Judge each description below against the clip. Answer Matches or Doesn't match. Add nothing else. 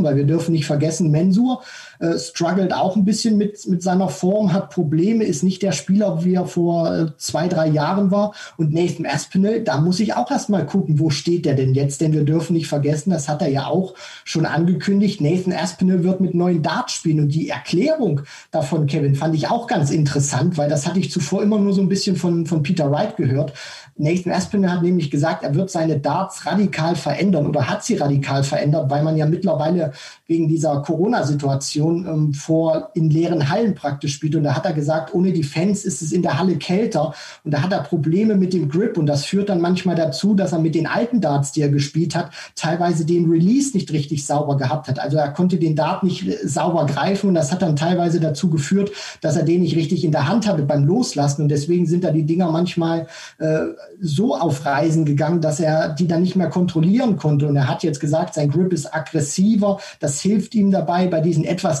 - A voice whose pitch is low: Doesn't match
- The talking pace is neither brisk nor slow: Doesn't match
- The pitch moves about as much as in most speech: Matches